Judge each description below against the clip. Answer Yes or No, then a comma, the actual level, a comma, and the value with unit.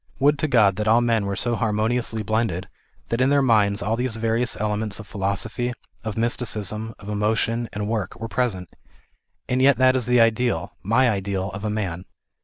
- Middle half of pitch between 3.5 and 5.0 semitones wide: No, narrow, 2.6 semitones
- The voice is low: Yes, low, 110 Hz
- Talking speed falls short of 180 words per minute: No, average, 190 wpm